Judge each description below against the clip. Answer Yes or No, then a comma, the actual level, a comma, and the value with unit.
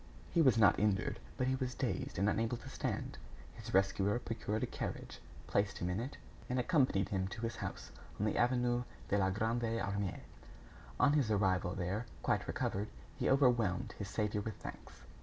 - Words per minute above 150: Yes, average, 180 wpm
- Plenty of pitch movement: No, average, 3.7 semitones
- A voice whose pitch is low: Yes, low, 110 Hz